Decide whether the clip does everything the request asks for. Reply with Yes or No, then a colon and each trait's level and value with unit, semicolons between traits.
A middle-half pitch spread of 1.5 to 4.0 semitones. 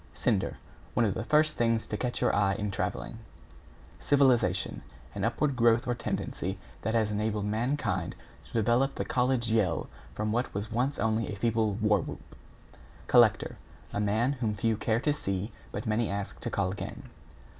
Yes: average, 2.7 semitones